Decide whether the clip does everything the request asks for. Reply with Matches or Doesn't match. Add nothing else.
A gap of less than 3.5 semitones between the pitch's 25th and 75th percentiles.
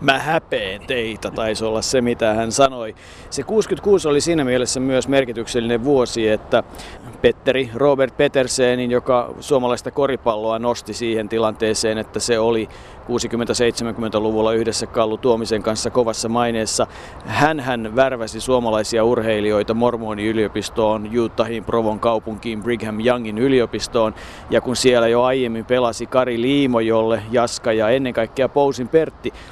Matches